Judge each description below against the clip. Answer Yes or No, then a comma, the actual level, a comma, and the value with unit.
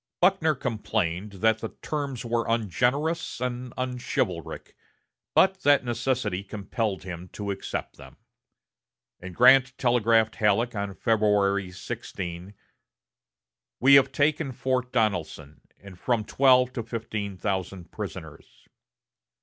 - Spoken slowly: Yes, slow, 110 wpm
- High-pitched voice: No, low, 115 Hz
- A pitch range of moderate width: Yes, average, 4.5 semitones